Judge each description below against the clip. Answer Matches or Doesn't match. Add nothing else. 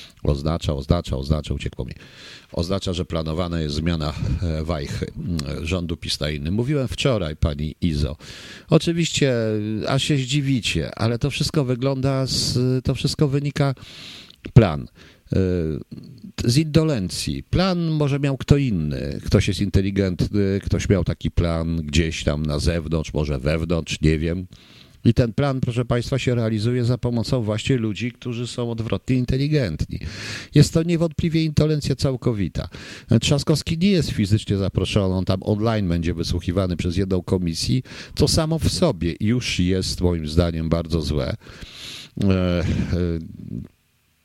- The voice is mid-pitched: Doesn't match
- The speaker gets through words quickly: Doesn't match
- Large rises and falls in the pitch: Matches